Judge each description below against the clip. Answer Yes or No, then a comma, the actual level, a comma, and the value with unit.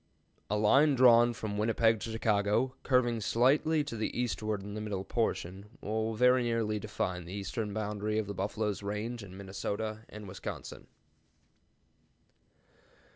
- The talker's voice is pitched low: Yes, low, 110 Hz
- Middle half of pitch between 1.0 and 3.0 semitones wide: Yes, narrow, 2.4 semitones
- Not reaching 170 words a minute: Yes, average, 140 wpm